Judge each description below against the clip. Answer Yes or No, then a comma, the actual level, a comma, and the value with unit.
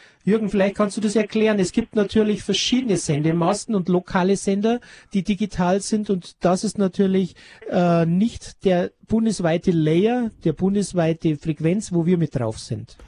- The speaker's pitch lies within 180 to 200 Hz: Yes, high, 190 Hz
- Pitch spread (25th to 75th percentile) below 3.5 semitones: No, average, 3.8 semitones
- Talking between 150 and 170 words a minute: Yes, average, 155 wpm